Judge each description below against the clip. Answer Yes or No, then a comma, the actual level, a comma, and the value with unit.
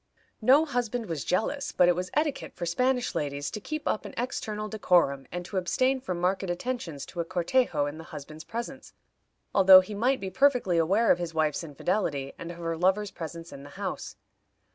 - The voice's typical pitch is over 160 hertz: Yes, medium, 185 Hz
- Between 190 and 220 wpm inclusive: Yes, average, 195 wpm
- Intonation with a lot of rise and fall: Yes, wide, 6.1 semitones